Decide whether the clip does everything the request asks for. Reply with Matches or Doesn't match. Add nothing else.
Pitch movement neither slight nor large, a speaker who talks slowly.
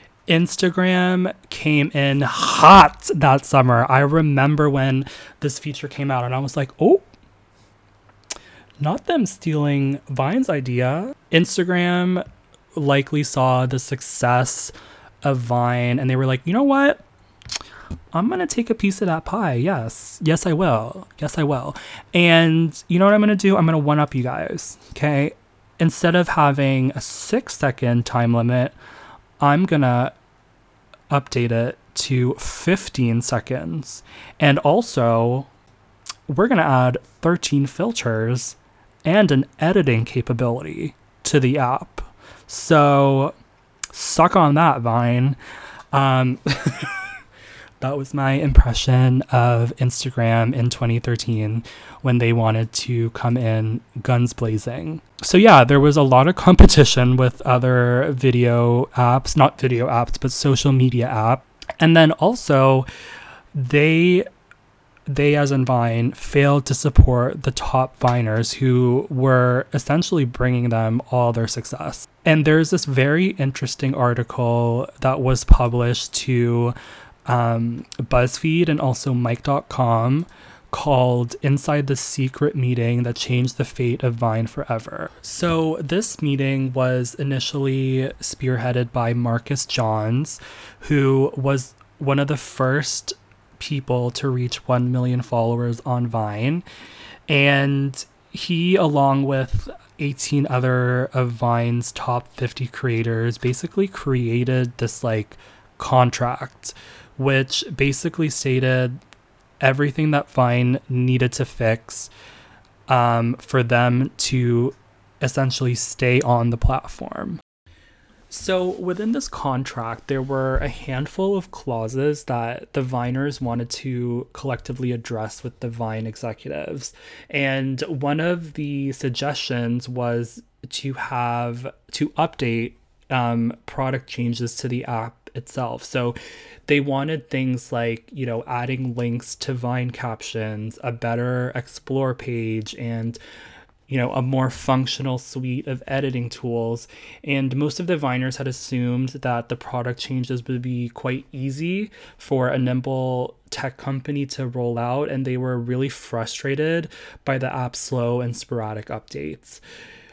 Matches